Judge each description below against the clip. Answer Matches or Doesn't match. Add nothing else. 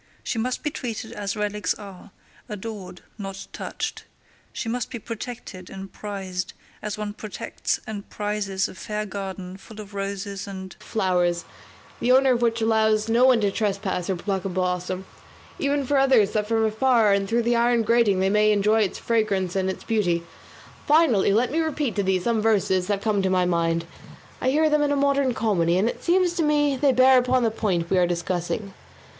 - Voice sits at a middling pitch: Doesn't match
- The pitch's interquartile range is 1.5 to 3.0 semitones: Doesn't match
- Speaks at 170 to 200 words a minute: Matches